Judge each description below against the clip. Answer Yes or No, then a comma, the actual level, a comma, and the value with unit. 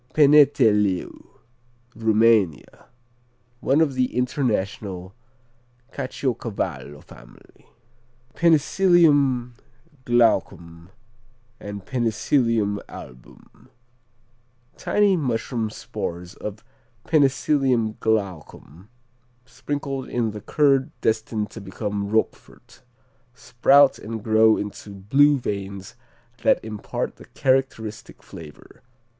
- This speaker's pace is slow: Yes, slow, 80 wpm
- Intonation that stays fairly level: No, average, 4.8 semitones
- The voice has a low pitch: Yes, low, 115 Hz